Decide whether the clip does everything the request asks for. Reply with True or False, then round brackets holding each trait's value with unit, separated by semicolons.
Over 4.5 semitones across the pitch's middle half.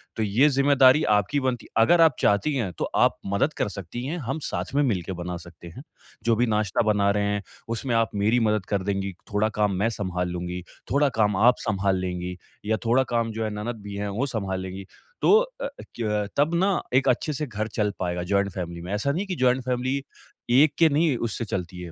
True (4.9 semitones)